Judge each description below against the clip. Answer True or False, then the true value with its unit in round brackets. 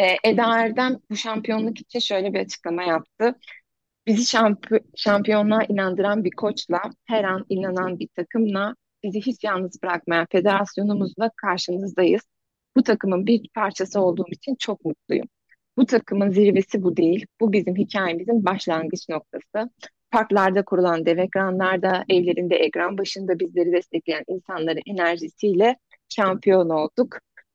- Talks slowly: False (125 wpm)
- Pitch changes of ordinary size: True (3.4 semitones)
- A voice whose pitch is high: True (195 Hz)